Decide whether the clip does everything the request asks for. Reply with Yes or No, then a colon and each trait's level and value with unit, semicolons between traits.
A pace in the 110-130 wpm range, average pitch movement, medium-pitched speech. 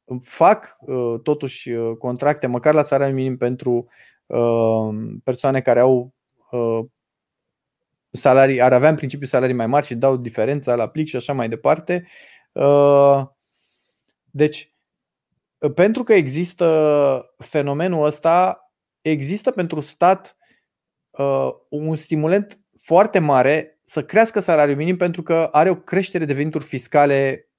Yes: slow, 115 wpm; average, 3.8 semitones; medium, 145 Hz